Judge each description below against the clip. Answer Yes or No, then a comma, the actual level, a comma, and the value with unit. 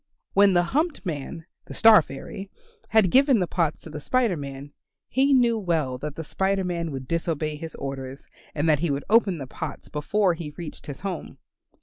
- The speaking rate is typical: Yes, average, 195 wpm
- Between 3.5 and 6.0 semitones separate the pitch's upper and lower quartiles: Yes, average, 5.1 semitones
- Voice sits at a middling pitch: Yes, medium, 165 Hz